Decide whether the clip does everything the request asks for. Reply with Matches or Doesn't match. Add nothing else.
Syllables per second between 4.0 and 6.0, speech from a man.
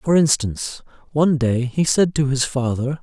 Matches